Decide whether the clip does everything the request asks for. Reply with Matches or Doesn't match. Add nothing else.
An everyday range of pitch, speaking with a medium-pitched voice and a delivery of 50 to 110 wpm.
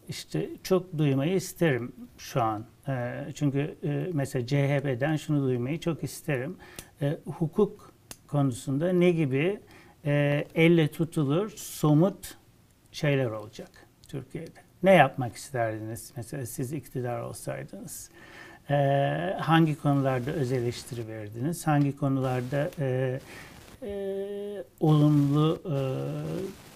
Matches